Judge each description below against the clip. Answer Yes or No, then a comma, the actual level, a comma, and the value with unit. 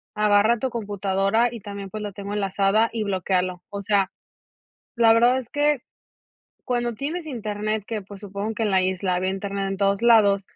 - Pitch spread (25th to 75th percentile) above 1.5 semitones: Yes, narrow, 2.6 semitones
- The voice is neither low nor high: No, high, 205 Hz